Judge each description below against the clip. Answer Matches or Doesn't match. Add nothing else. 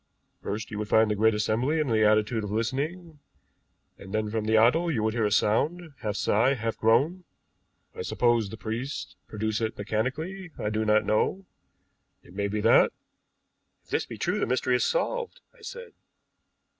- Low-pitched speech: Matches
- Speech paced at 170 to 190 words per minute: Matches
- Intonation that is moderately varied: Doesn't match